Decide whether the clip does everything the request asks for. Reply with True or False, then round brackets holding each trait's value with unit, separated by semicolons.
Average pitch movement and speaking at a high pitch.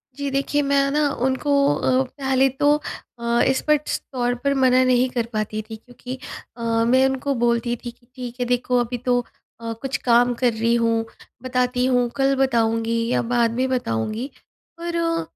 False (2.2 semitones; 250 Hz)